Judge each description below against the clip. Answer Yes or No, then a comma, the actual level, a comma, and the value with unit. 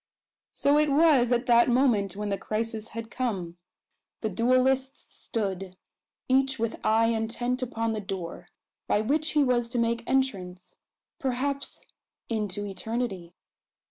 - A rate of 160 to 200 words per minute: No, slow, 135 wpm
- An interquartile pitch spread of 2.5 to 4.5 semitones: Yes, average, 3.7 semitones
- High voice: Yes, high, 230 Hz